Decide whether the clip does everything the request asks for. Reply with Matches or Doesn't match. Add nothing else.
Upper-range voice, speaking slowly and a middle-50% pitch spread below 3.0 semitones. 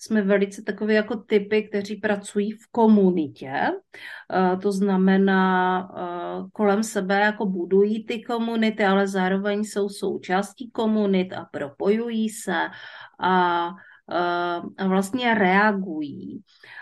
Matches